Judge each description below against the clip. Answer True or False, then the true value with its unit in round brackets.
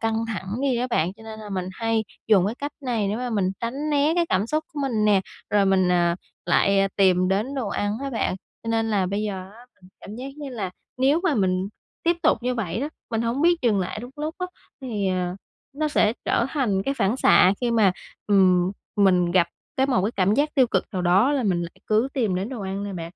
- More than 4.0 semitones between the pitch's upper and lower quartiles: True (4.9 semitones)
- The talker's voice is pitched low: False (215 Hz)